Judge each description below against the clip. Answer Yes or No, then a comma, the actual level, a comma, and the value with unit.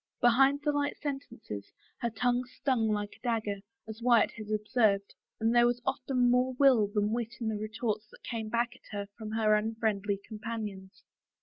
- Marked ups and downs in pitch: No, narrow, 2.5 semitones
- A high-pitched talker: Yes, high, 225 Hz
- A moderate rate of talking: Yes, average, 180 wpm